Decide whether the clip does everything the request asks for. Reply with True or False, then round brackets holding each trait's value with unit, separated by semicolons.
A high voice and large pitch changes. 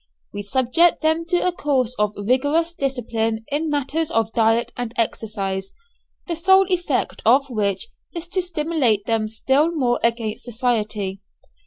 True (250 Hz; 6.3 semitones)